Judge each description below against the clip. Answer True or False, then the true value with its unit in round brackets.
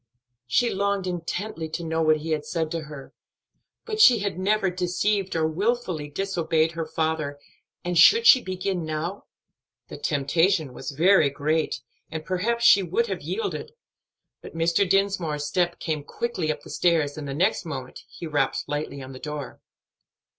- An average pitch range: True (4.1 semitones)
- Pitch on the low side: False (165 Hz)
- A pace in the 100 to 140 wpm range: False (165 wpm)